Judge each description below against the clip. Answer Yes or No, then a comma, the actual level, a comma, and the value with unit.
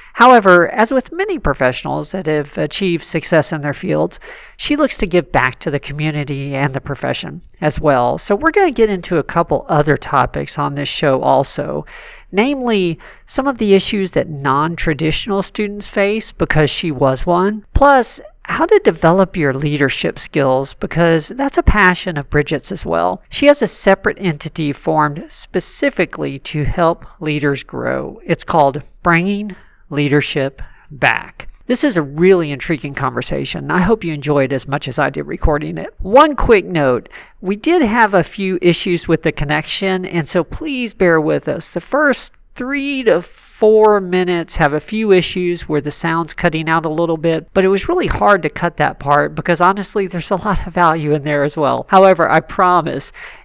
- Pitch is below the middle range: No, medium, 175 Hz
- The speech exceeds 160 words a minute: Yes, average, 180 wpm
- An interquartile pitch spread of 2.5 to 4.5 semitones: No, average, 5.2 semitones